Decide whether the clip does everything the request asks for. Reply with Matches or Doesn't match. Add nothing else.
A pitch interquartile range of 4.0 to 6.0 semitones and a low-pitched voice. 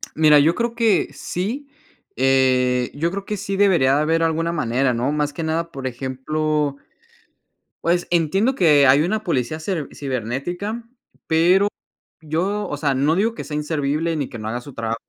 Doesn't match